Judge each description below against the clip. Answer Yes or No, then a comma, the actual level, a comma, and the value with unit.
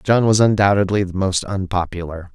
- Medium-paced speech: Yes, average, 155 wpm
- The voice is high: No, very low, 95 Hz